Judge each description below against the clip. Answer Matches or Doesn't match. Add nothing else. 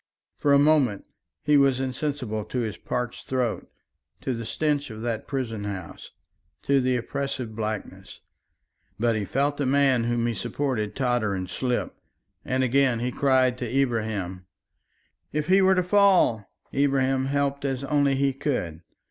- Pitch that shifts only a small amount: Doesn't match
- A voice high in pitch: Doesn't match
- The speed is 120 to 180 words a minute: Matches